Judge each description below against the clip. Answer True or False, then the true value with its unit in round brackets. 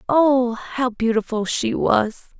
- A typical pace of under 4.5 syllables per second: True (3.3 syllables/s)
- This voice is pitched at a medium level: False (240 Hz)